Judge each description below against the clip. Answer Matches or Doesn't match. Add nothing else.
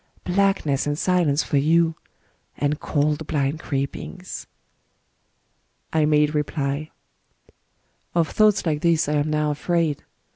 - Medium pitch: Matches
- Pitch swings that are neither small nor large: Doesn't match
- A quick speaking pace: Doesn't match